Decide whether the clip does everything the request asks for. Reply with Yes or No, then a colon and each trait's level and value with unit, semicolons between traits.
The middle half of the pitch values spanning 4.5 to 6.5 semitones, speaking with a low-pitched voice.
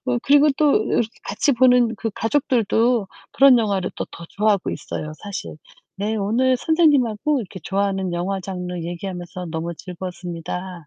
No: wide, 5.5 semitones; high, 200 Hz